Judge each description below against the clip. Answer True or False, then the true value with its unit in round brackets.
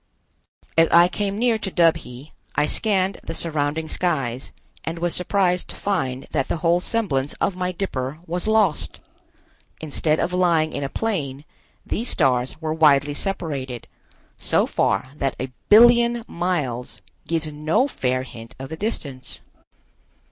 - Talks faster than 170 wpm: False (145 wpm)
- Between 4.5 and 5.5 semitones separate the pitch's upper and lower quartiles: True (5.2 semitones)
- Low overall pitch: False (160 Hz)